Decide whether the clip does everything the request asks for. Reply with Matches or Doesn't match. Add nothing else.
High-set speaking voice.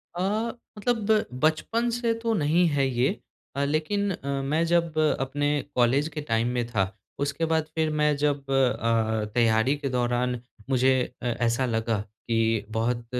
Doesn't match